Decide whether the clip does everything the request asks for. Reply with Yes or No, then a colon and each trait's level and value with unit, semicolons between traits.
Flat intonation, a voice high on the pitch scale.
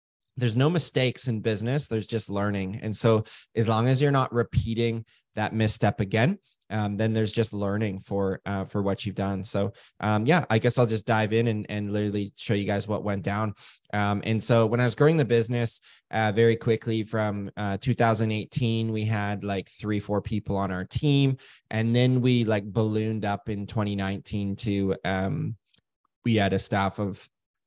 No: narrow, 2.3 semitones; low, 110 Hz